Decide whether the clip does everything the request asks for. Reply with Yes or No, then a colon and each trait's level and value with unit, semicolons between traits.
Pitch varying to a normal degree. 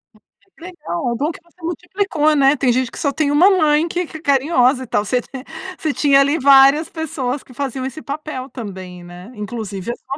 Yes: average, 4.0 semitones